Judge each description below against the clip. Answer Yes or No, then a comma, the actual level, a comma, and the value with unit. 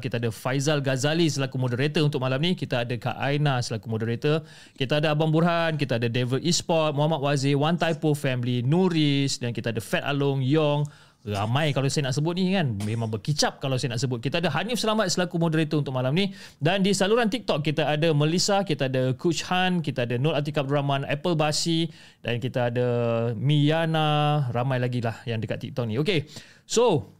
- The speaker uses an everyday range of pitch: Yes, average, 4.1 semitones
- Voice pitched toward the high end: No, medium, 145 Hz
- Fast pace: Yes, fast, 195 wpm